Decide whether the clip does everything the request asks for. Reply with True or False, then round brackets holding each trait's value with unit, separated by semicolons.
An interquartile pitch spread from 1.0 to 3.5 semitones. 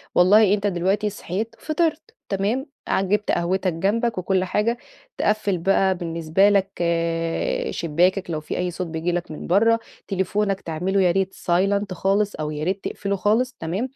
True (3.1 semitones)